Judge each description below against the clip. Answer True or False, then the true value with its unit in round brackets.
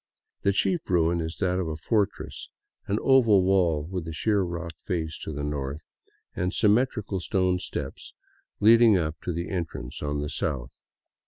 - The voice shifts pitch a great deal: False (3.9 semitones)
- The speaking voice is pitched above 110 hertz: False (90 Hz)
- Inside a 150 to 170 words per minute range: True (165 wpm)